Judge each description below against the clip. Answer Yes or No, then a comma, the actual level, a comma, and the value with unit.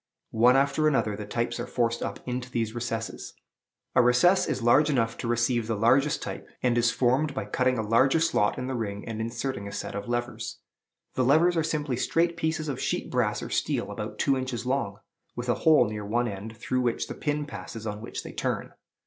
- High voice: No, low, 120 Hz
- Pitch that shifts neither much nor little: Yes, average, 3.3 semitones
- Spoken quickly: Yes, fast, 215 wpm